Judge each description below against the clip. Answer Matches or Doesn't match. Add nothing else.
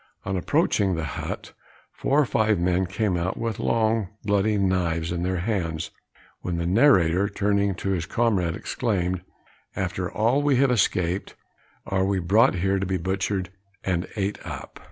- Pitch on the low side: Matches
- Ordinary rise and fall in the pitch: Matches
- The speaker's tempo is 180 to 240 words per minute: Doesn't match